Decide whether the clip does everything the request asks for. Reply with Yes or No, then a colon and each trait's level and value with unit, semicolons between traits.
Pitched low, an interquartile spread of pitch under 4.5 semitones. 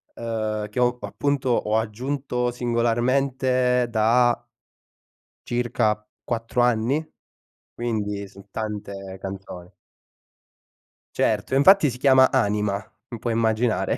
Yes: low, 120 Hz; average, 2.8 semitones